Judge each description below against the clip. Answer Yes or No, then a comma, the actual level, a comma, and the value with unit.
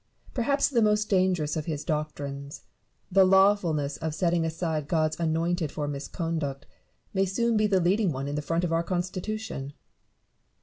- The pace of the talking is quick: No, average, 160 wpm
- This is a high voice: No, medium, 170 Hz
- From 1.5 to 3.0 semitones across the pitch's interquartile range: No, average, 4.2 semitones